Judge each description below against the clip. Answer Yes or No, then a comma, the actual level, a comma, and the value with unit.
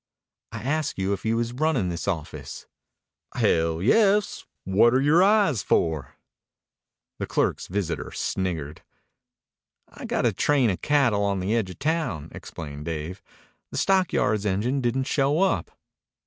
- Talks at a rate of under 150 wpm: Yes, average, 140 wpm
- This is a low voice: Yes, low, 110 Hz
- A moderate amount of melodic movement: No, wide, 8.0 semitones